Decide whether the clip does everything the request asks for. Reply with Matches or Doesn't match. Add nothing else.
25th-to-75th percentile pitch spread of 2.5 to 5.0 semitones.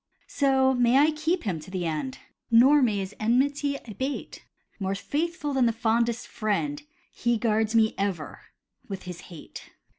Doesn't match